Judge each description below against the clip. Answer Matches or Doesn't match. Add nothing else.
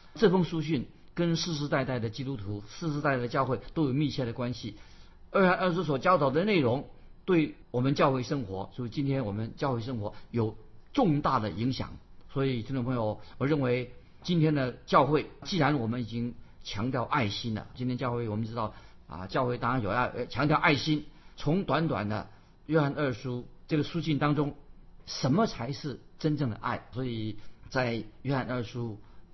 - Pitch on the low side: Matches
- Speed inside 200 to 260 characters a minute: Doesn't match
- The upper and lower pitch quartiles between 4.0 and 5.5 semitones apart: Matches